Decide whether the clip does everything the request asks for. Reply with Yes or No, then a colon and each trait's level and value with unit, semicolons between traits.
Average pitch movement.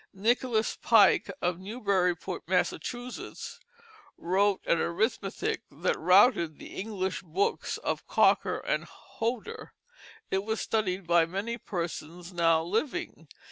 Yes: average, 4.4 semitones